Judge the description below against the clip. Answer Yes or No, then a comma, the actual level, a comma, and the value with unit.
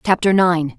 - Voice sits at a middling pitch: Yes, medium, 170 Hz